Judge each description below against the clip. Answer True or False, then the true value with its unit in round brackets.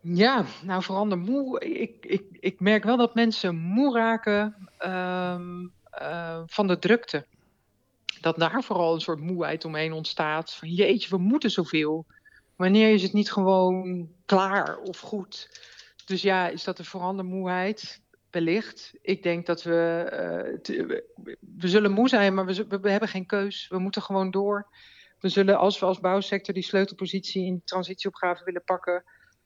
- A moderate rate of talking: True (170 wpm)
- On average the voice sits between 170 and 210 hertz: True (190 Hz)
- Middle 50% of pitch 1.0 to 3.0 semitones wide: True (2.4 semitones)